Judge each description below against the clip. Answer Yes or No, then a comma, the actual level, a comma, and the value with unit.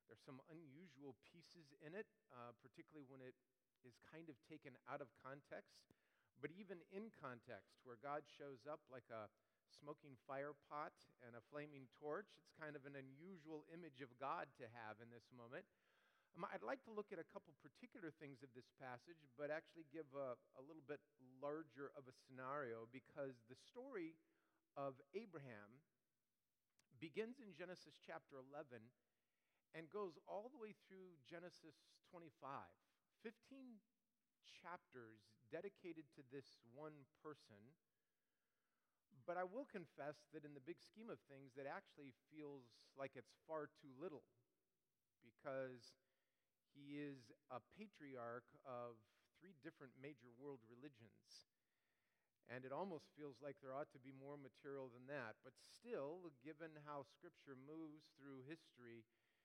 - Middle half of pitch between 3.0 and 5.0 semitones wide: Yes, average, 3.7 semitones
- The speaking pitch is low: No, medium, 145 Hz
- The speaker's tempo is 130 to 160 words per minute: Yes, average, 150 wpm